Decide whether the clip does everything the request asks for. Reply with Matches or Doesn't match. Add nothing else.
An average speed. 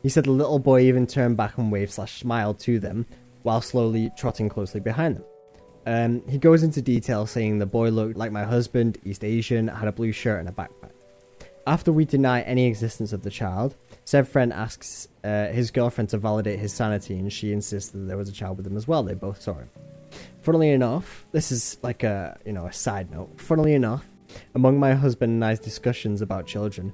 Doesn't match